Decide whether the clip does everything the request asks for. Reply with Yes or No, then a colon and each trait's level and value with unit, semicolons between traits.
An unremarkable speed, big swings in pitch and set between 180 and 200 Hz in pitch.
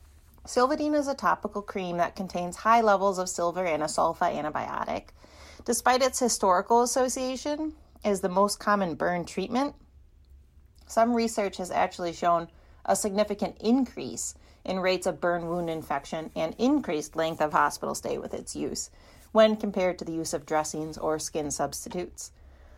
Yes: average, 155 wpm; wide, 6.0 semitones; medium, 185 Hz